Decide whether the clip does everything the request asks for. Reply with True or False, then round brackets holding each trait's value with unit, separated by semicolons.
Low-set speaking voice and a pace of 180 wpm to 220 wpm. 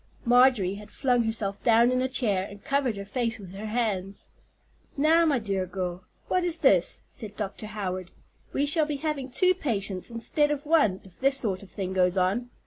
False (225 Hz; 195 wpm)